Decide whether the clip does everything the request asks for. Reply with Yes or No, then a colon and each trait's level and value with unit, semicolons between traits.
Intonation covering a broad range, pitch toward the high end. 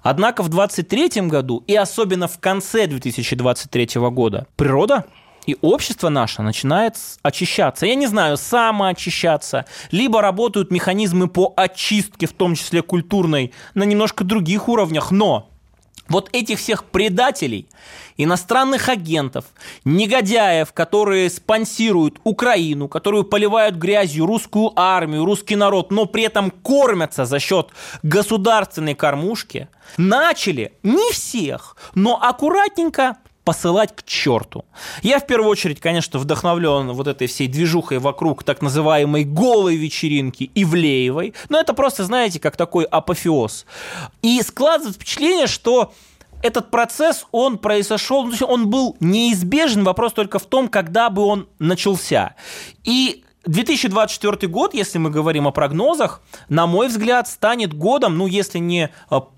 Yes: wide, 5.8 semitones; high, 195 Hz